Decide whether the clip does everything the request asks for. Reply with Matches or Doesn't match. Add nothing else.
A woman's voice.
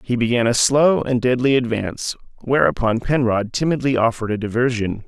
Doesn't match